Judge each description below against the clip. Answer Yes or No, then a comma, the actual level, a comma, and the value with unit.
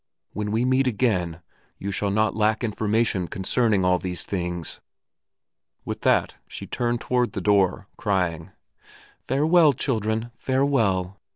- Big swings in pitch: No, average, 4.4 semitones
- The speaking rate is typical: No, slow, 125 wpm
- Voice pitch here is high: No, low, 105 Hz